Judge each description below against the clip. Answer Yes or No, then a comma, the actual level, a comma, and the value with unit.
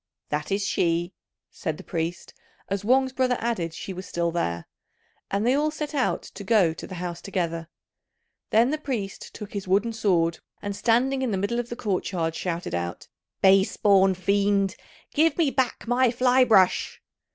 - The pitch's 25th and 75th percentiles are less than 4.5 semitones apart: No, wide, 5.6 semitones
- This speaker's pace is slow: No, average, 180 wpm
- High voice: Yes, high, 200 Hz